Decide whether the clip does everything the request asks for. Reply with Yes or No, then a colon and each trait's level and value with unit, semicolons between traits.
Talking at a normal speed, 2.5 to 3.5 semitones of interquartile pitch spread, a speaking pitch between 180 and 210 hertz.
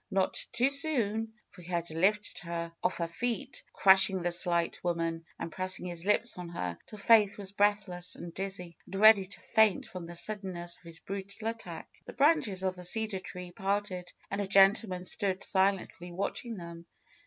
Yes: average, 190 wpm; average, 3.1 semitones; high, 190 Hz